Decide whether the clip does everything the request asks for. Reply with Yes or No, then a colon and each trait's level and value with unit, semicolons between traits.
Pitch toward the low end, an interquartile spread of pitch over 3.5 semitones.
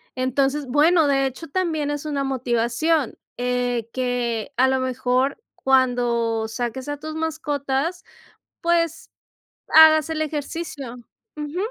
No: very high, 275 Hz; average, 3.9 semitones